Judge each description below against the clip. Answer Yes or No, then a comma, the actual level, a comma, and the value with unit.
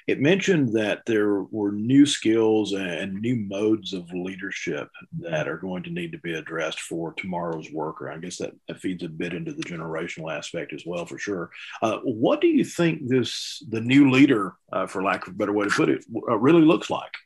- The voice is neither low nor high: No, low, 110 Hz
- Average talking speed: No, fast, 210 wpm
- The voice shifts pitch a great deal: Yes, wide, 5.9 semitones